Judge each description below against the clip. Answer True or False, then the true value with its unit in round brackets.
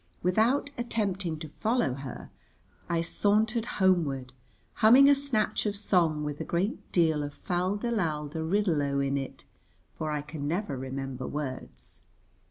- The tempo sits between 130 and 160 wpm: True (155 wpm)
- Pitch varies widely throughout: True (6.4 semitones)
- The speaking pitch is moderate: True (170 Hz)